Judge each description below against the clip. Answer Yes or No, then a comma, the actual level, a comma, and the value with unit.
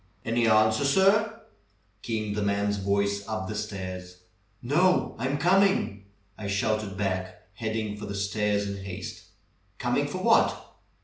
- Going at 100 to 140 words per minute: Yes, slow, 135 wpm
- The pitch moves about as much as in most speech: No, narrow, 2.3 semitones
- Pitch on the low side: Yes, low, 105 Hz